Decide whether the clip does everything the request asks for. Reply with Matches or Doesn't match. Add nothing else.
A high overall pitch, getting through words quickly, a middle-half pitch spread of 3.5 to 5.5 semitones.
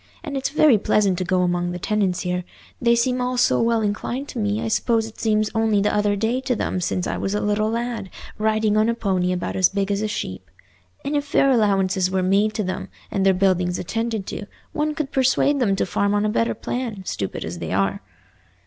Matches